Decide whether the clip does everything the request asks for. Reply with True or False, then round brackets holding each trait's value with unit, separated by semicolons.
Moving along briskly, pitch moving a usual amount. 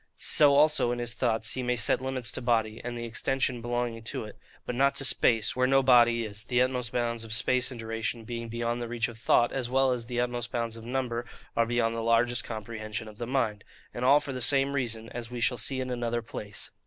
False (240 wpm; 1.8 semitones)